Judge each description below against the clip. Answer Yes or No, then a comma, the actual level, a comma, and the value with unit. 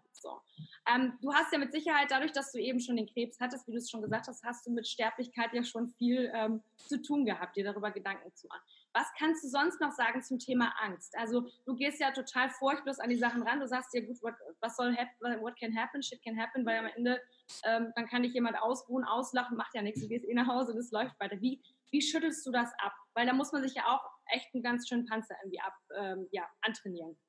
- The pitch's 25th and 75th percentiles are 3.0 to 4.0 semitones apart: No, narrow, 2.4 semitones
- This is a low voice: No, high, 240 Hz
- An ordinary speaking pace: No, fast, 250 wpm